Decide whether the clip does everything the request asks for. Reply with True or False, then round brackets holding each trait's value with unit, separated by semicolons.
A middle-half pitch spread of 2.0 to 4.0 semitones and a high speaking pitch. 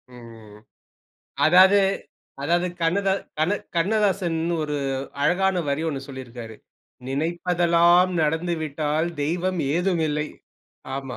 False (3.4 semitones; 165 Hz)